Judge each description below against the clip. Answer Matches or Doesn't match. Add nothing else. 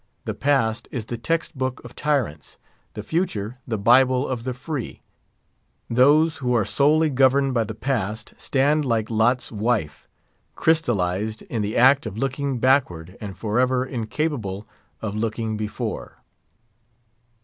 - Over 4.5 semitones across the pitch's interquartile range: Doesn't match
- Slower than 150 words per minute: Matches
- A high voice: Doesn't match